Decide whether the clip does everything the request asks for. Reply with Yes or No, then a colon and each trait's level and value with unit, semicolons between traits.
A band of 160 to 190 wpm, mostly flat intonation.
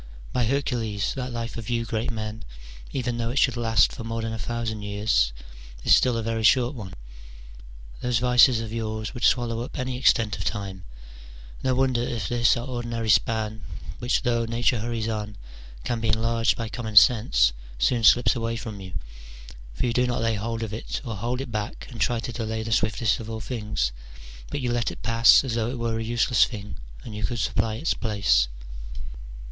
No: average, 200 wpm; narrow, 1.8 semitones